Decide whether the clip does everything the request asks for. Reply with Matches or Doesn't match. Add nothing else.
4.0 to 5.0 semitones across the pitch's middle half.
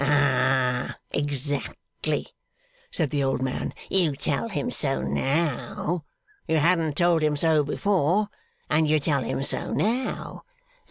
Doesn't match